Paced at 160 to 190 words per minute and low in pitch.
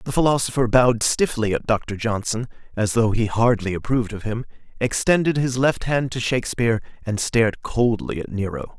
Yes: average, 170 wpm; low, 115 Hz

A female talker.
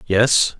No: male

